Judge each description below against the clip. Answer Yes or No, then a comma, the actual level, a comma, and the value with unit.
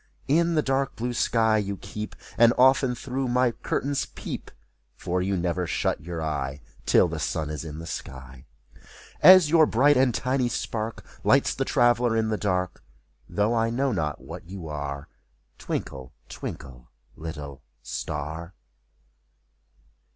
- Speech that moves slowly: No, average, 145 wpm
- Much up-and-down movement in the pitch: Yes, wide, 8.0 semitones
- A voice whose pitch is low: Yes, low, 105 Hz